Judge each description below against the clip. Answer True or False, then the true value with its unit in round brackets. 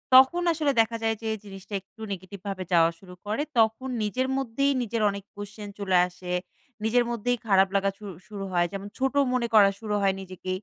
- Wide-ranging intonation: False (3.3 semitones)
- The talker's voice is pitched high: True (210 Hz)